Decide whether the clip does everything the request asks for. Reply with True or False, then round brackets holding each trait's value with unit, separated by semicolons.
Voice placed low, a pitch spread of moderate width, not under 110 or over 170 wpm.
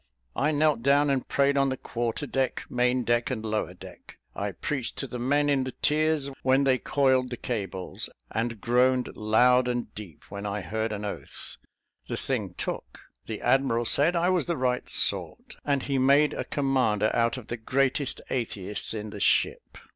False (125 Hz; 3.6 semitones; 185 wpm)